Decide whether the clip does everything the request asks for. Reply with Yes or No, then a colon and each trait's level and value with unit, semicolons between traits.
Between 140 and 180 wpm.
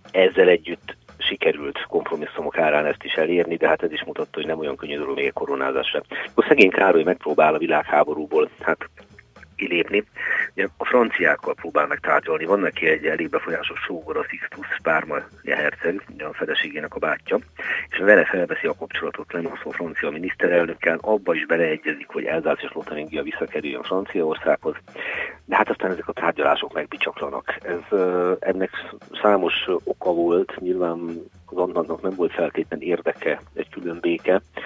Yes: average, 150 wpm